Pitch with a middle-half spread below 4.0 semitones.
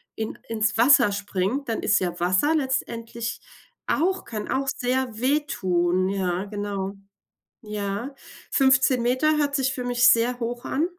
No: average, 4.6 semitones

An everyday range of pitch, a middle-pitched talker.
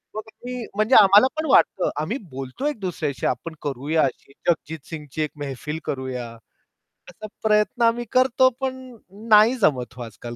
No: wide, 9.0 semitones; medium, 170 Hz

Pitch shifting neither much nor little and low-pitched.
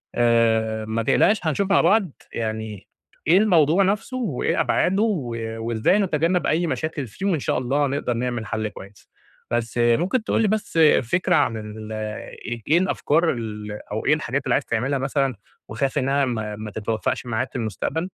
No: wide, 7.3 semitones; low, 130 Hz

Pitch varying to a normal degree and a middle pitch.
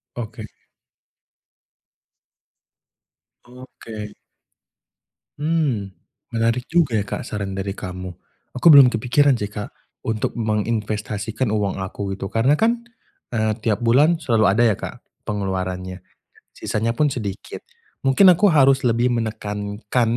No: average, 3.8 semitones; low, 110 Hz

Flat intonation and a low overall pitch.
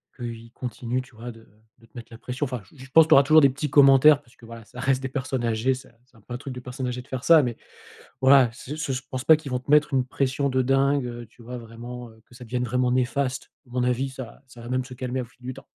Yes: narrow, 1.9 semitones; low, 130 Hz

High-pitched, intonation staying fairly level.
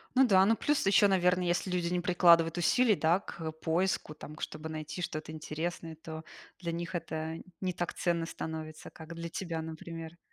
No: medium, 170 Hz; narrow, 2.1 semitones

